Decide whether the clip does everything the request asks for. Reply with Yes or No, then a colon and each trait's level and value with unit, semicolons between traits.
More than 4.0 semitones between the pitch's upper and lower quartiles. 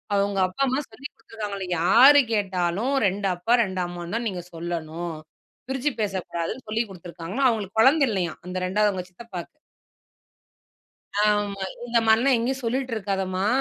Yes: average, 4.4 semitones